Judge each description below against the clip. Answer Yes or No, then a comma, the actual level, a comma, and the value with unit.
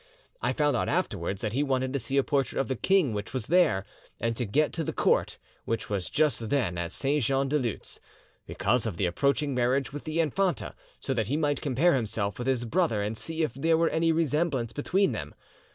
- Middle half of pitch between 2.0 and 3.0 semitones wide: No, average, 5.1 semitones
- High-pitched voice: No, low, 135 Hz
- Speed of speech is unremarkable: No, fast, 220 wpm